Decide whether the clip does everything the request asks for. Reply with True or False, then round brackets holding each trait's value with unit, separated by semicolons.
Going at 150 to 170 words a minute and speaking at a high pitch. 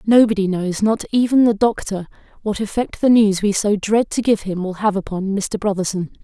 False (200 wpm; 205 Hz)